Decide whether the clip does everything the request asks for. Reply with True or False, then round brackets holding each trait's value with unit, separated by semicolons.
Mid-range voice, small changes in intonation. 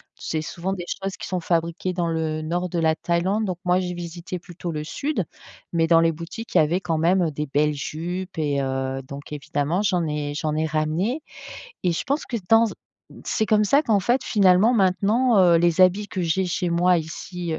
False (175 Hz; 3.2 semitones)